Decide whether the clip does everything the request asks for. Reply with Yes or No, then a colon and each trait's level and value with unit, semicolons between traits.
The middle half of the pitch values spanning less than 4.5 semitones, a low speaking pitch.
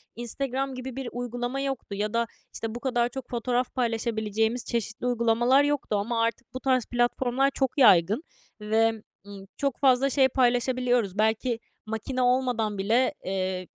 No: narrow, 2.6 semitones; high, 240 Hz